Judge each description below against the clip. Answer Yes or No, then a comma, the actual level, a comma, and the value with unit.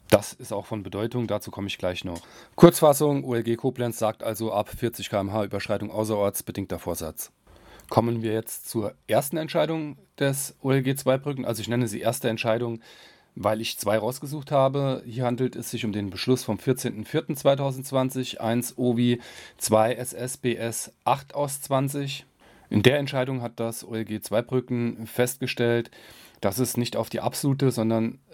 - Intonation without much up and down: No, average, 3.1 semitones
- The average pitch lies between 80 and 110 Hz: No, low, 120 Hz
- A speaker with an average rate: Yes, average, 155 wpm